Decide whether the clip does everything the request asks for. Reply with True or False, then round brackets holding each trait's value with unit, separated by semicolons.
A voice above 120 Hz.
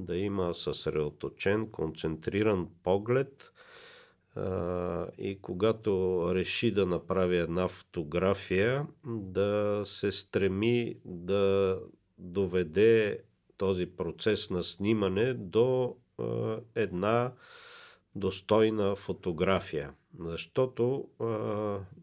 False (100 Hz)